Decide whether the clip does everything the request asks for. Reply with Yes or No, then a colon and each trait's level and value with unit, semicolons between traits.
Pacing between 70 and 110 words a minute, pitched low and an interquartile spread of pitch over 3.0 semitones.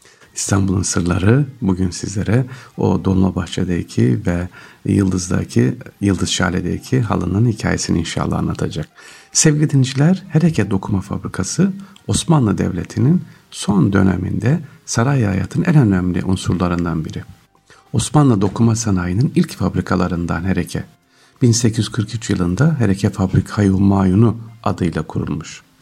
Yes: average, 100 wpm; low, 100 Hz; wide, 5.4 semitones